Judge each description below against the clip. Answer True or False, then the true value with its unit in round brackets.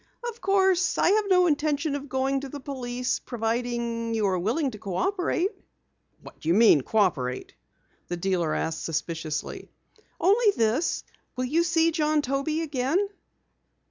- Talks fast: False (140 wpm)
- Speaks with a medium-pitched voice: False (265 Hz)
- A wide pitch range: True (7.1 semitones)